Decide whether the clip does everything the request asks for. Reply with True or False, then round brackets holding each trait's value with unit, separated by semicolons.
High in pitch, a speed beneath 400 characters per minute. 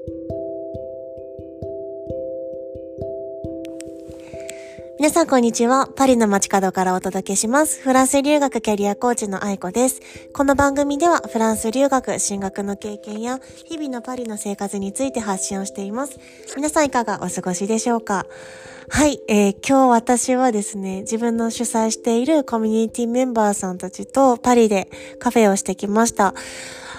True (215 Hz; 310 characters per minute)